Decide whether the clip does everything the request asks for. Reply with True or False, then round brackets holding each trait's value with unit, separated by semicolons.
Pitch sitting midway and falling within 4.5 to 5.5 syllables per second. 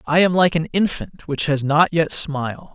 True (155 Hz; 4.7 syllables/s)